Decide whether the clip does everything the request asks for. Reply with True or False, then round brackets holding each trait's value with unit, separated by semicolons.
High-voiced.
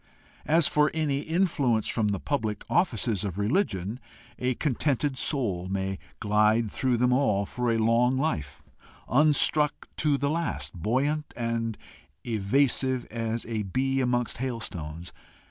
False (120 Hz)